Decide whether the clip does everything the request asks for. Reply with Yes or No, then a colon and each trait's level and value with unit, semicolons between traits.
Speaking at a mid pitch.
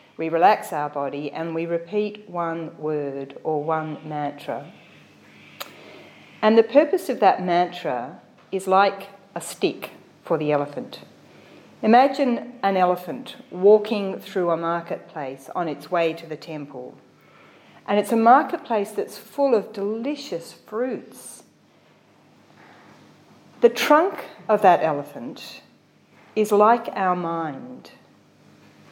Yes: medium, 180 Hz